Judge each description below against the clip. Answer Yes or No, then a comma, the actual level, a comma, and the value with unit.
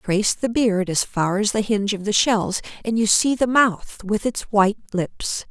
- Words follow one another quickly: Yes, fast, 220 wpm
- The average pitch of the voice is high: Yes, high, 210 Hz